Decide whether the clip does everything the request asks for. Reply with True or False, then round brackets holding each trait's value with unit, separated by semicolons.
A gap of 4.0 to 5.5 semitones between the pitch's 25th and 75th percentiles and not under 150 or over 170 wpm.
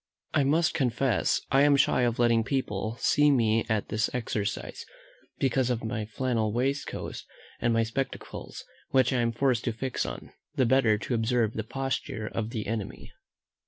False (3.1 semitones; 165 wpm)